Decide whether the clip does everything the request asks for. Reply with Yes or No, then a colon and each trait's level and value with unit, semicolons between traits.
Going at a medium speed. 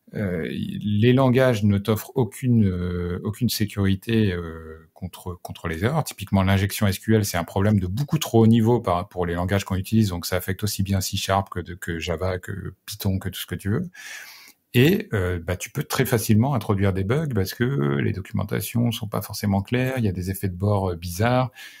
Yes: average, 210 wpm